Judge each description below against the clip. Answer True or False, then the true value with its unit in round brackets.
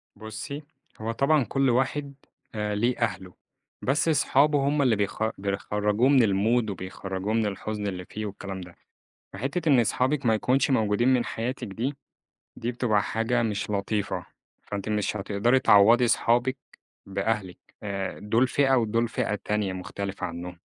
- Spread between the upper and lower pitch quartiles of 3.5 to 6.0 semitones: True (4.2 semitones)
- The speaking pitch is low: True (110 Hz)